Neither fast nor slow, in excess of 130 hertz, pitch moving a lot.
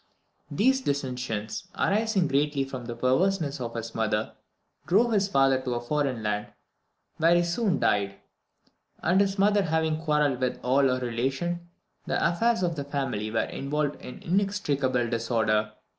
Yes: average, 150 wpm; medium, 140 Hz; wide, 6.2 semitones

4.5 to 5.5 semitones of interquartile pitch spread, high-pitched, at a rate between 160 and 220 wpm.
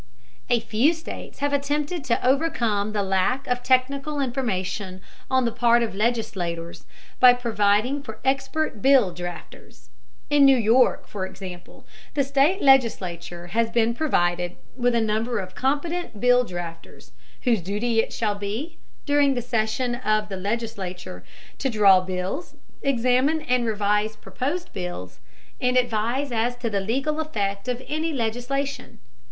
No: average, 4.9 semitones; high, 235 Hz; average, 145 wpm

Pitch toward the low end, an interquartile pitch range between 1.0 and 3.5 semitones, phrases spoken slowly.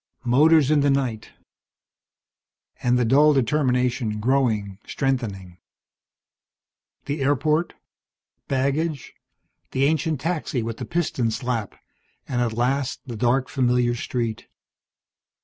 Yes: low, 130 Hz; average, 3.2 semitones; slow, 105 wpm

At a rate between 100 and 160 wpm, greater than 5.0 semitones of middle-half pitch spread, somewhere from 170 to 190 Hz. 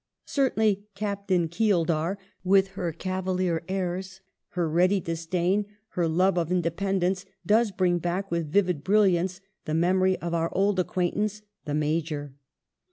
No: slow, 135 wpm; narrow, 2.5 semitones; medium, 185 Hz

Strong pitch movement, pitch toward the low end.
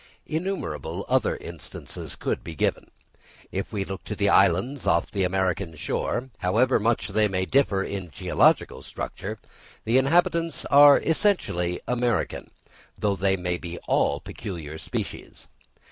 Yes: wide, 6.8 semitones; low, 100 Hz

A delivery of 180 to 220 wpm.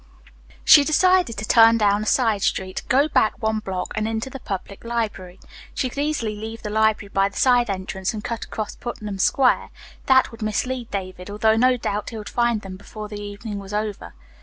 Yes: average, 200 wpm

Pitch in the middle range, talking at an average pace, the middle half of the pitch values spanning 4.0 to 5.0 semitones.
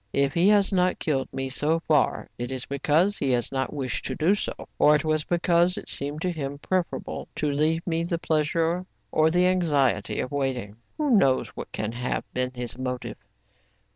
Yes: medium, 150 Hz; average, 195 wpm; average, 4.4 semitones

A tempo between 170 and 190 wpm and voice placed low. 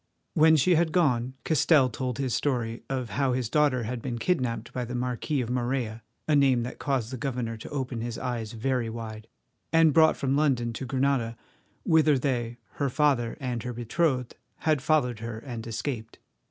Yes: average, 180 wpm; low, 125 Hz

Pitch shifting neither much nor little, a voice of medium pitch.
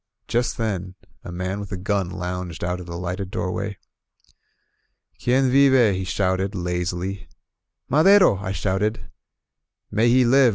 No: average, 4.2 semitones; very low, 95 Hz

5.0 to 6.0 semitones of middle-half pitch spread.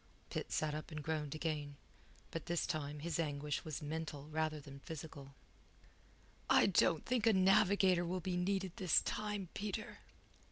No: average, 3.7 semitones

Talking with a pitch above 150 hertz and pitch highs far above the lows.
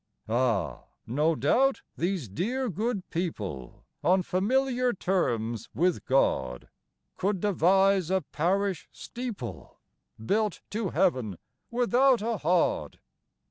Yes: medium, 185 Hz; wide, 8.6 semitones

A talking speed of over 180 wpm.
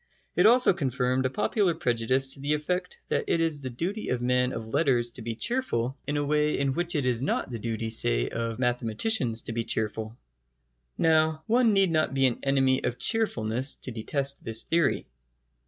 Yes: average, 190 wpm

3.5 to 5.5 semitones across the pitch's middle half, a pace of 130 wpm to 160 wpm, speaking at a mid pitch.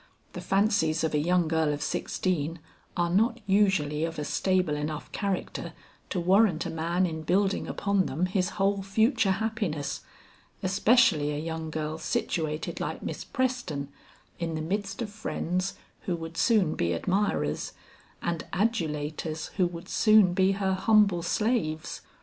Yes: average, 4.1 semitones; average, 150 wpm; medium, 180 Hz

